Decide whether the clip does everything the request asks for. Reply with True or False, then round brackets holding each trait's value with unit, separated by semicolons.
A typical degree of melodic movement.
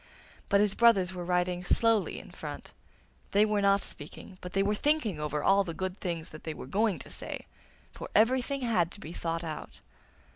True (3.6 semitones)